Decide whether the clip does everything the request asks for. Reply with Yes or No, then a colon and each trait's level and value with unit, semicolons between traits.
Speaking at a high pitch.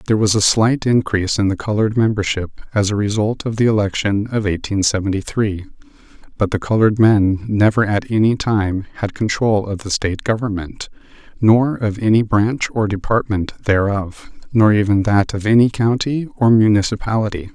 No: low, 105 Hz